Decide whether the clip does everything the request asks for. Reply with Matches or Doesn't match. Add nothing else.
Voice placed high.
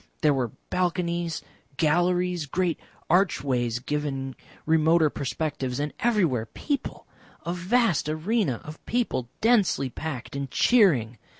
Doesn't match